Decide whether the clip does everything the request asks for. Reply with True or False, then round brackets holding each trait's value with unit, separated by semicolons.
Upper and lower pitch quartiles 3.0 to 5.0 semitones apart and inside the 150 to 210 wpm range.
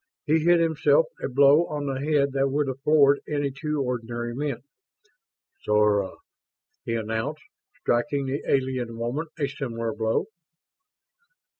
False (3.8 semitones; 135 wpm)